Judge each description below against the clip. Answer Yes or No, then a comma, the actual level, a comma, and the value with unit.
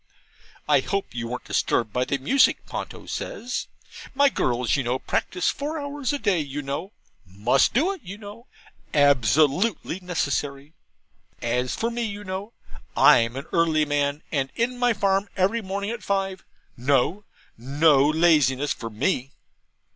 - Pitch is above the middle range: No, medium, 160 Hz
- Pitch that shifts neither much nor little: No, wide, 7.3 semitones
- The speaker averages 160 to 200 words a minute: No, average, 150 wpm